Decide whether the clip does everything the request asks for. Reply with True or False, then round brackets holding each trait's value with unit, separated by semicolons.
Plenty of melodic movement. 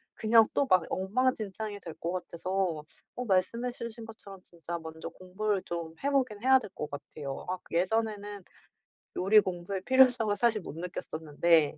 False (4.5 semitones)